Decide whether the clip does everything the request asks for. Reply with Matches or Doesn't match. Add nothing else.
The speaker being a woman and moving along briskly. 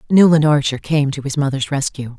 Doesn't match